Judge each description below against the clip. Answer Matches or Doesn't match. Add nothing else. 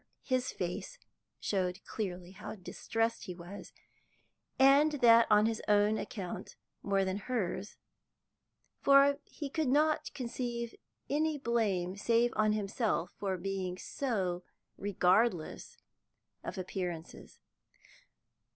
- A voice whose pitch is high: Matches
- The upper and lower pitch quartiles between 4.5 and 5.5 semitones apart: Matches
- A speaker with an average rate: Doesn't match